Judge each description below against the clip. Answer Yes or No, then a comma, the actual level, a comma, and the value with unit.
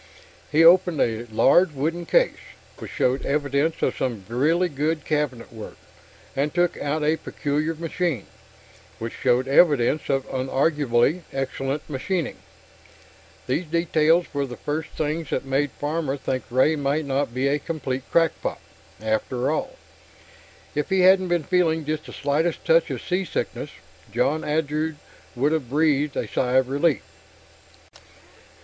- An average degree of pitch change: Yes, average, 3.3 semitones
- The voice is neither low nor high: Yes, medium, 150 Hz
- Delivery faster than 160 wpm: No, average, 140 wpm